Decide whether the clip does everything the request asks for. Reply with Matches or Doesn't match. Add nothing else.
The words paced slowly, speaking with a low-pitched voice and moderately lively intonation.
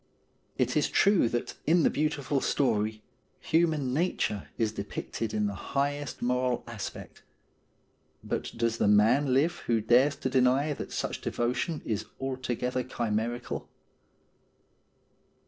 Matches